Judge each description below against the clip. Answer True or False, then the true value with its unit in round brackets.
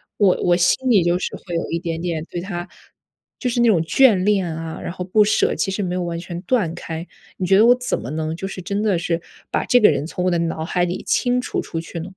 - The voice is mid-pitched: True (180 Hz)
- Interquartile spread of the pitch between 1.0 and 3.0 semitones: False (3.5 semitones)